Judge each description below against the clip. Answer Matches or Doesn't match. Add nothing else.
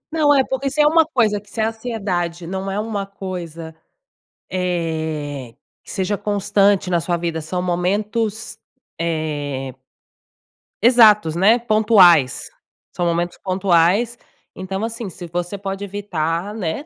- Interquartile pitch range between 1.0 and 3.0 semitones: Doesn't match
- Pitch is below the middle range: Doesn't match